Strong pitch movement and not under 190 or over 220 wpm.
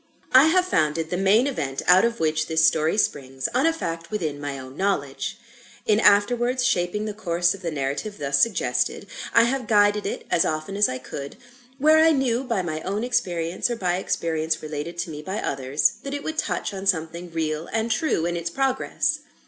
Yes: wide, 6.6 semitones; average, 200 wpm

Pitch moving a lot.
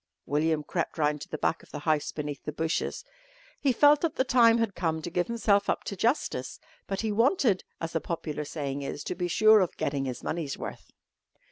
Yes: wide, 6.8 semitones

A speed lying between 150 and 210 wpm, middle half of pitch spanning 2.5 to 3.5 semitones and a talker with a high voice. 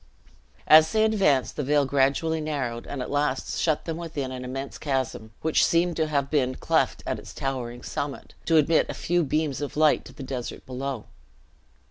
No: average, 185 wpm; average, 3.2 semitones; medium, 145 Hz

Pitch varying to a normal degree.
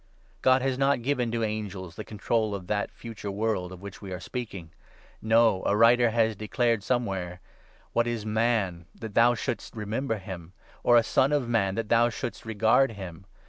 Yes: average, 3.1 semitones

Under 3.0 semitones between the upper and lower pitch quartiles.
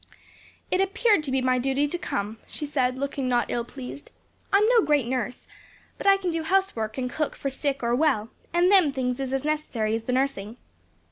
No: average, 4.1 semitones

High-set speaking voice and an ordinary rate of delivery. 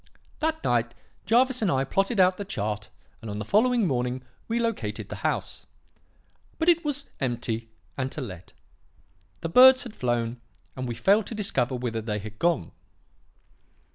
No: low, 135 Hz; average, 165 wpm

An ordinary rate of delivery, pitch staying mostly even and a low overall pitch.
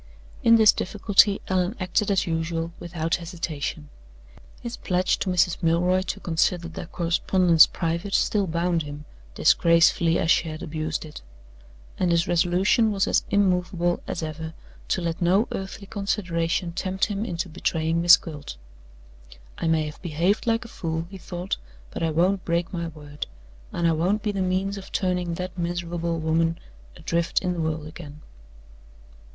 No: average, 160 wpm; narrow, 2.3 semitones; medium, 175 Hz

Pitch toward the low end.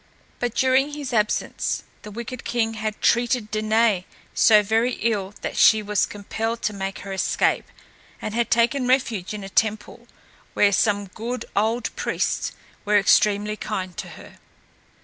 No: high, 215 Hz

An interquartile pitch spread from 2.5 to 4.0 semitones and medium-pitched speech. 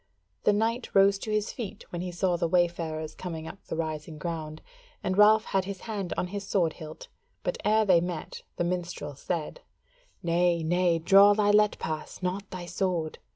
Yes: average, 3.2 semitones; medium, 180 Hz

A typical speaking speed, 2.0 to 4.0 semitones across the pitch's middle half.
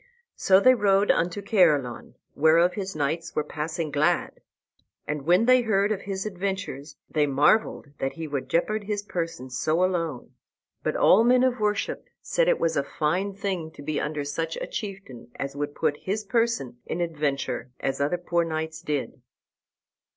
No: average, 170 wpm; average, 5.3 semitones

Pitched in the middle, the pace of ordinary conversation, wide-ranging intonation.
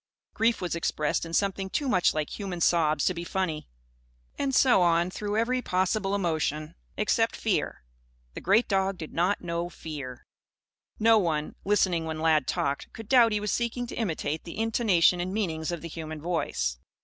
No: medium, 180 Hz; average, 175 wpm; average, 4.6 semitones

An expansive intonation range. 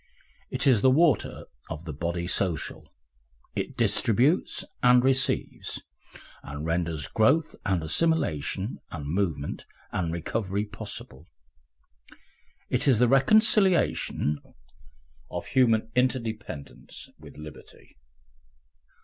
Yes: wide, 8.0 semitones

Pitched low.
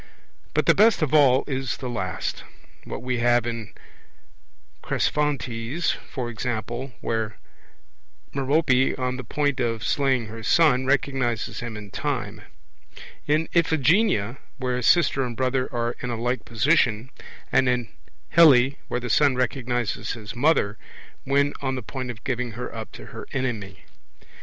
Yes: low, 125 Hz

